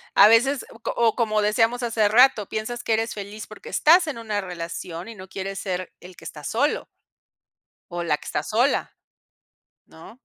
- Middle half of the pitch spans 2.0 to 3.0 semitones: No, average, 3.7 semitones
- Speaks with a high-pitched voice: Yes, high, 215 Hz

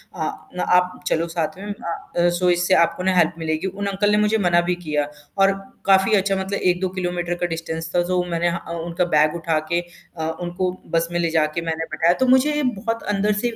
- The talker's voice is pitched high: No, medium, 175 Hz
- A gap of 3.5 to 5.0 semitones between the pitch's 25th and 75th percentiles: No, average, 2.7 semitones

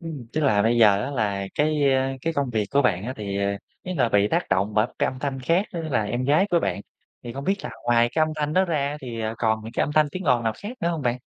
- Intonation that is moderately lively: No, wide, 5.8 semitones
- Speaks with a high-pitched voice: No, low, 130 Hz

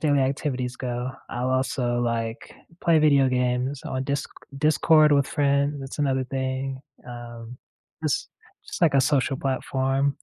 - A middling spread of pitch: No, narrow, 2.0 semitones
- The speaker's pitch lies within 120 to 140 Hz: Yes, low, 135 Hz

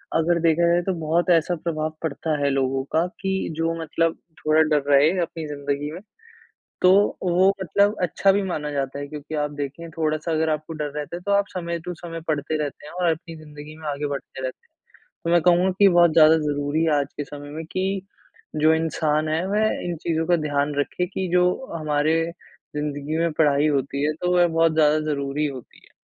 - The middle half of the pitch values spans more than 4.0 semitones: No, average, 2.7 semitones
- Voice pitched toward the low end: No, medium, 155 Hz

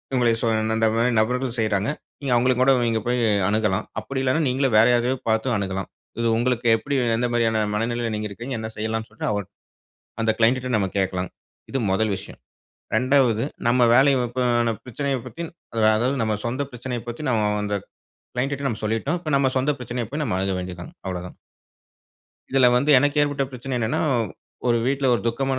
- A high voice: No, low, 120 Hz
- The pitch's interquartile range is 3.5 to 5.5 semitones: No, average, 3.1 semitones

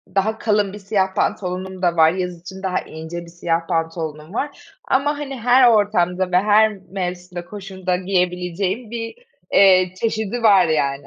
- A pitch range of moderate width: Yes, average, 3.0 semitones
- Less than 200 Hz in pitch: Yes, medium, 185 Hz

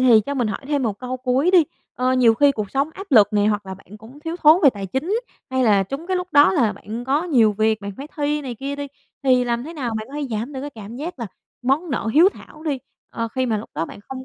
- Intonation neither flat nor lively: Yes, average, 4.8 semitones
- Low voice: No, very high, 255 Hz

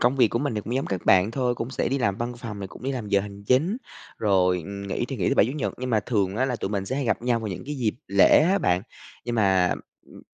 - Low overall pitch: Yes, low, 115 Hz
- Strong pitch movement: No, average, 4.3 semitones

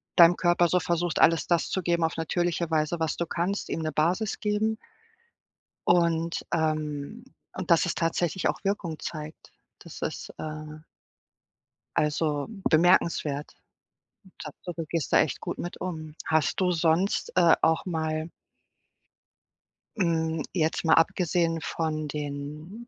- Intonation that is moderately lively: No, narrow, 1.9 semitones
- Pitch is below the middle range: No, medium, 165 Hz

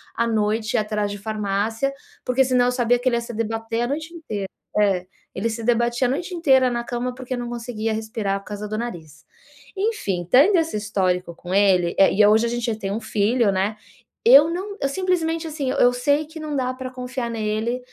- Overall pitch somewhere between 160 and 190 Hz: No, high, 235 Hz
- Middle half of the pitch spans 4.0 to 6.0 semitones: No, average, 3.6 semitones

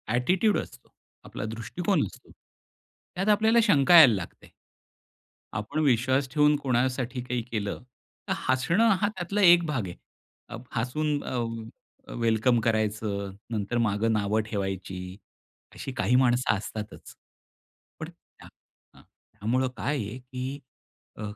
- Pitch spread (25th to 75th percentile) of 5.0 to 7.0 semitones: Yes, average, 5.3 semitones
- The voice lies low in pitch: Yes, low, 125 Hz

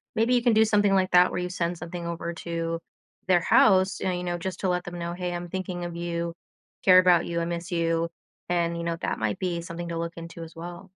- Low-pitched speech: No, medium, 175 Hz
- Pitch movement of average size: No, narrow, 1.4 semitones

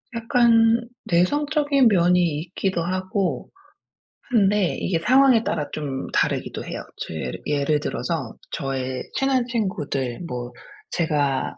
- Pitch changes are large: Yes, wide, 8.3 semitones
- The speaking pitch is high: No, medium, 180 Hz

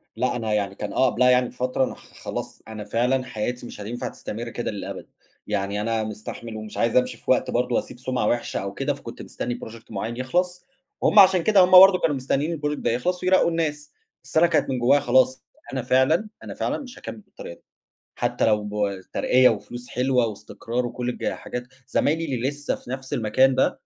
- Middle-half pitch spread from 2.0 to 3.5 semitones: No, average, 3.9 semitones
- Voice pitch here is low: Yes, low, 125 Hz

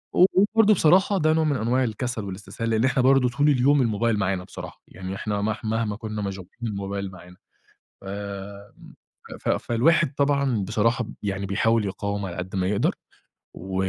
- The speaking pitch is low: Yes, low, 110 Hz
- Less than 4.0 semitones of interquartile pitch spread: No, average, 4.9 semitones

